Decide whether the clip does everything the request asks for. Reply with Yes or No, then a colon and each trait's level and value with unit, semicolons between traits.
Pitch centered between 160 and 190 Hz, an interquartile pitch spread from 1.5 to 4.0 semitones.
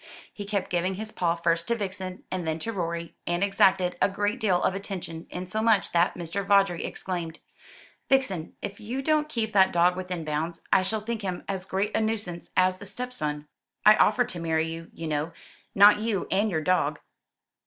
Yes: medium, 185 Hz; average, 3.6 semitones